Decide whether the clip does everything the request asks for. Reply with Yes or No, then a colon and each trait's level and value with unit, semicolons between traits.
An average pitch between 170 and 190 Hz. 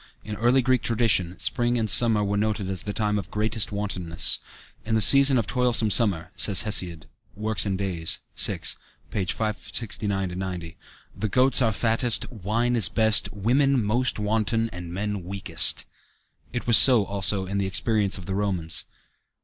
No: low, 105 Hz